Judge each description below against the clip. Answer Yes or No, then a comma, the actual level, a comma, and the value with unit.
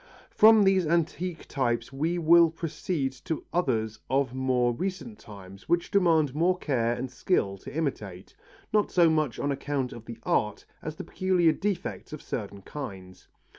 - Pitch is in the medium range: Yes, medium, 150 Hz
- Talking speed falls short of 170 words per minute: Yes, average, 160 wpm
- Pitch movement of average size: No, wide, 6.4 semitones